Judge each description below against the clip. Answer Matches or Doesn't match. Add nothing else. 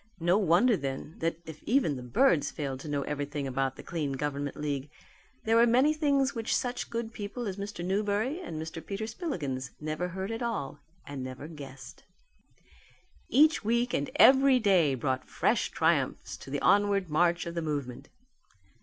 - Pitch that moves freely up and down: Matches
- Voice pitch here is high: Doesn't match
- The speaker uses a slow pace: Doesn't match